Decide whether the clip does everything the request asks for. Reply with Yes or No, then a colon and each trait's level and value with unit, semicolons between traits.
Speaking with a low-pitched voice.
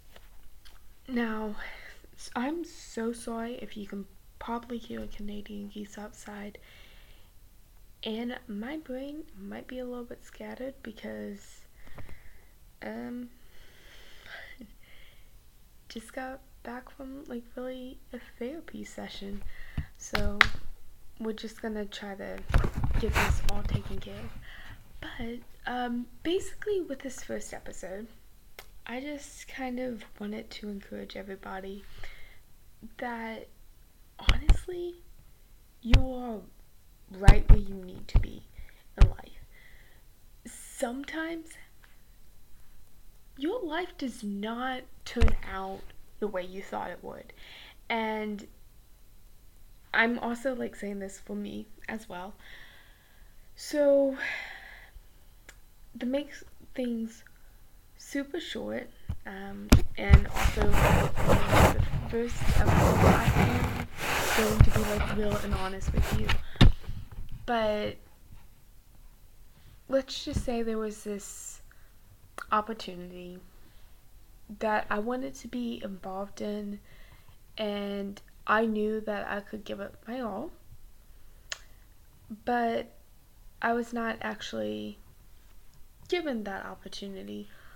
No: high, 215 Hz